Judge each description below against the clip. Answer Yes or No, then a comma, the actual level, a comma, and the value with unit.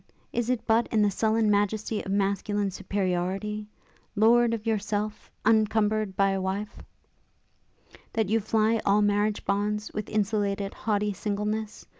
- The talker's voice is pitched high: Yes, high, 210 Hz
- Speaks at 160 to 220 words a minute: No, slow, 135 wpm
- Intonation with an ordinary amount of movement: No, narrow, 1.4 semitones